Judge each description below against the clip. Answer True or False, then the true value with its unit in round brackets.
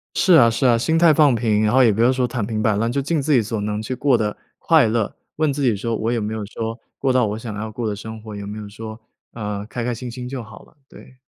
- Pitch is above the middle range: False (115 Hz)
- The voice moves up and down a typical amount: True (3.1 semitones)